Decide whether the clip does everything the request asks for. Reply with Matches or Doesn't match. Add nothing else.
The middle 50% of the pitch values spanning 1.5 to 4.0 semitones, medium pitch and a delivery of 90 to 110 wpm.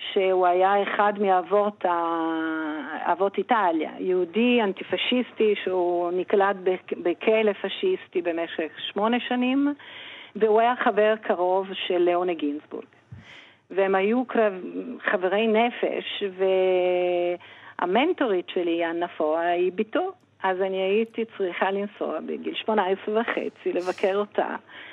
Doesn't match